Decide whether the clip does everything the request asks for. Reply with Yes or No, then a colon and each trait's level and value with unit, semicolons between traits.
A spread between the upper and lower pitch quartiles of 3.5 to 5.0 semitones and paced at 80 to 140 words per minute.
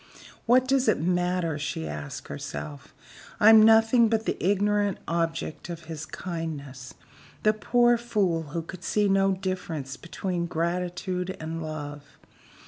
Yes: average, 4.5 semitones; slow, 135 wpm